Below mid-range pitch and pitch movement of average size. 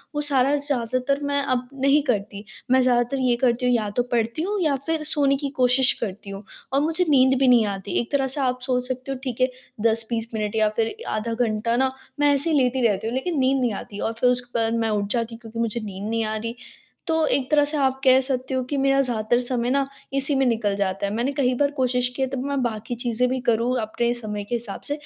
No: very high, 250 Hz; average, 3.1 semitones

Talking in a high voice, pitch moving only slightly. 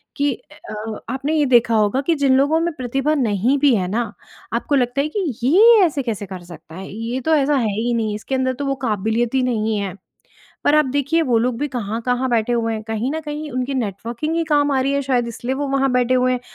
No: very high, 255 Hz; average, 4.0 semitones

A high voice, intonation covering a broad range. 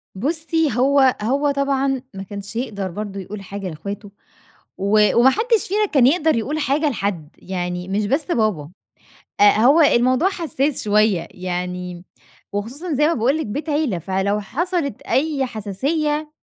Yes: high, 240 Hz; wide, 6.9 semitones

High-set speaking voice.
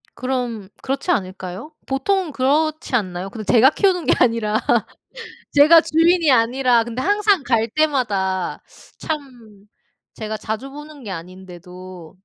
Yes: very high, 250 Hz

